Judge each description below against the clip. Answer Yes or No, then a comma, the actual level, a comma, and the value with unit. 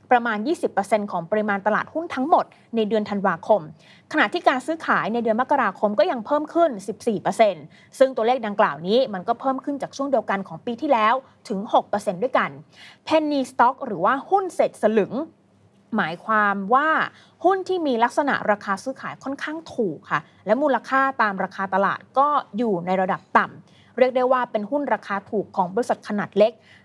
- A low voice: No, high, 230 Hz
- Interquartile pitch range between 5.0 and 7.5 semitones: Yes, wide, 5.4 semitones